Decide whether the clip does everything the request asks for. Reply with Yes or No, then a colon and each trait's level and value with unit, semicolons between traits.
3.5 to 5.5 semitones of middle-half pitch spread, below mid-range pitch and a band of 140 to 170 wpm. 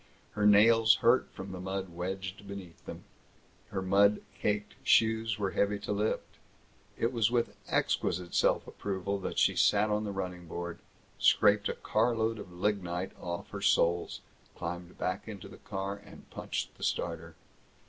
No: average, 2.7 semitones; low, 100 Hz; average, 160 wpm